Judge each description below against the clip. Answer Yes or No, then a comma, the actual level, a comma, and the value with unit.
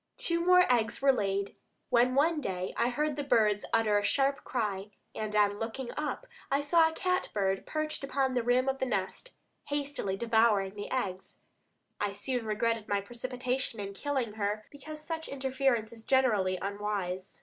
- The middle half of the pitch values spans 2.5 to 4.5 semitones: No, average, 5.1 semitones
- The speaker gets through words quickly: No, average, 170 wpm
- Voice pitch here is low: No, high, 235 Hz